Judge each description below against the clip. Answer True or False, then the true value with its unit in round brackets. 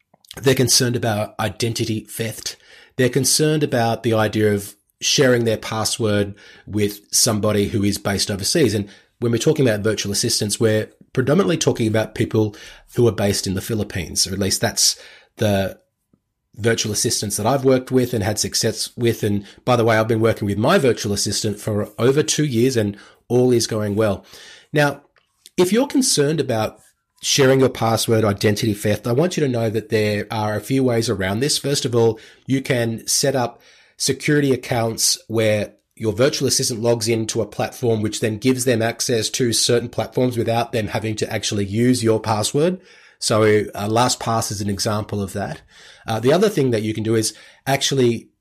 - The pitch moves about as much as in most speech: True (3.0 semitones)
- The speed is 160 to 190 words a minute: True (185 wpm)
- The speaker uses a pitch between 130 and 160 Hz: False (115 Hz)